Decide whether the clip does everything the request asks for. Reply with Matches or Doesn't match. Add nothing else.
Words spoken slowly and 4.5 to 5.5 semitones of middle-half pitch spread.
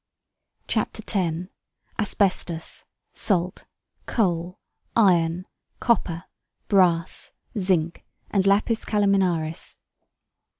Doesn't match